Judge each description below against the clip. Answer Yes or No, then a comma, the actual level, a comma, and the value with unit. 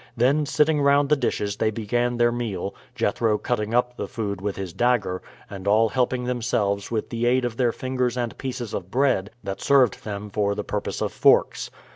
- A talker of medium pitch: No, low, 120 Hz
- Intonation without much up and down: No, average, 3.5 semitones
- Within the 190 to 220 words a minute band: Yes, average, 195 wpm